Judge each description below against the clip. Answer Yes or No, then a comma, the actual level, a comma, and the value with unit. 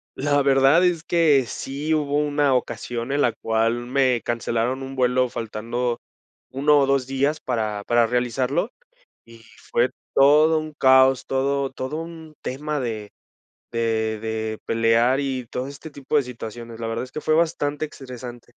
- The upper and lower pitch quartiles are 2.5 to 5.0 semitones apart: Yes, average, 3.4 semitones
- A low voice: Yes, low, 130 Hz